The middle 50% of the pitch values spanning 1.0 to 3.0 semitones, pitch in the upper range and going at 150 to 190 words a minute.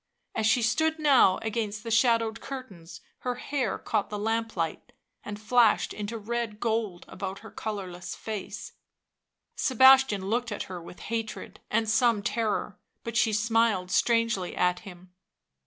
No: narrow, 2.5 semitones; high, 220 Hz; average, 140 wpm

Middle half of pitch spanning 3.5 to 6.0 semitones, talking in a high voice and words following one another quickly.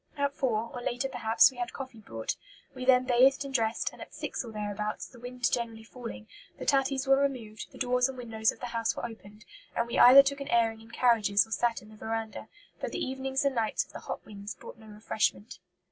No: average, 2.9 semitones; high, 235 Hz; fast, 230 wpm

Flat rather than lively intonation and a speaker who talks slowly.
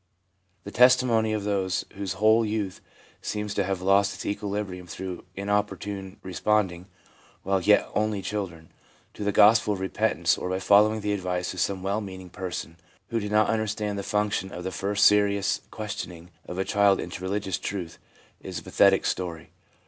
No: narrow, 2.0 semitones; average, 170 wpm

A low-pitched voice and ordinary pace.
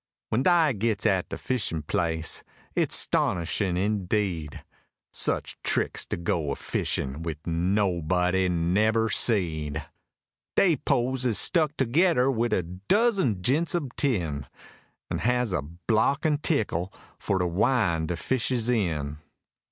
No: low, 100 Hz; slow, 130 wpm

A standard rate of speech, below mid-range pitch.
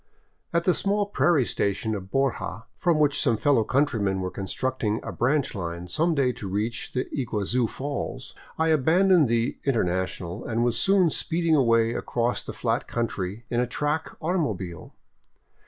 Yes: average, 160 wpm; low, 125 Hz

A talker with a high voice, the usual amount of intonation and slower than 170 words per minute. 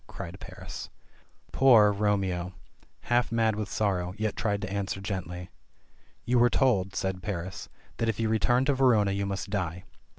No: low, 100 Hz; average, 3.1 semitones; average, 160 wpm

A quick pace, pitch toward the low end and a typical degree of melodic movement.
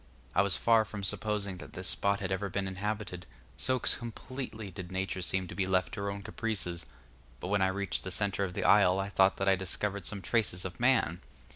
No: fast, 220 wpm; low, 100 Hz; narrow, 1.9 semitones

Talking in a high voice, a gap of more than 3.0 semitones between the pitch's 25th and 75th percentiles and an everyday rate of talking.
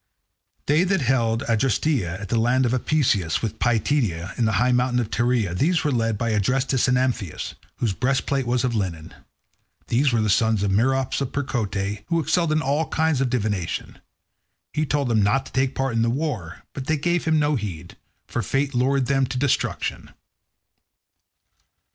No: low, 125 Hz; average, 4.1 semitones; average, 180 wpm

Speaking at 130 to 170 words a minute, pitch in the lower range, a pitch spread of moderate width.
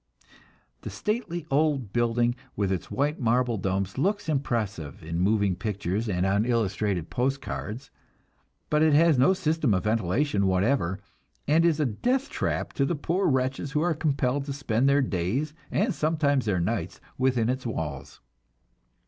No: average, 155 wpm; low, 125 Hz; wide, 6.7 semitones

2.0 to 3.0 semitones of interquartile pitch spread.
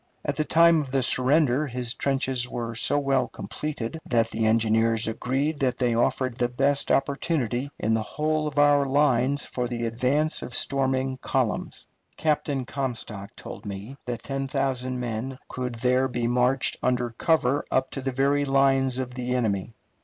Yes: narrow, 2.4 semitones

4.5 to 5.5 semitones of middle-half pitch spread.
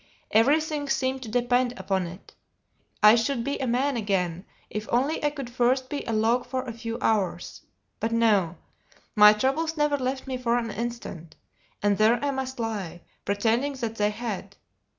No: average, 3.8 semitones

